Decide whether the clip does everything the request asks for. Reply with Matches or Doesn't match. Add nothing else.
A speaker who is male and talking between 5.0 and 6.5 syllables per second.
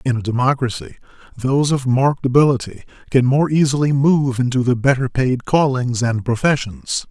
Matches